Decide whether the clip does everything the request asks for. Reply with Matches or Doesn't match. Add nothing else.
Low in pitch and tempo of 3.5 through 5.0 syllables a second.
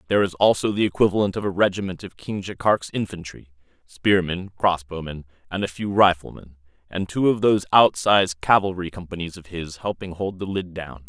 Doesn't match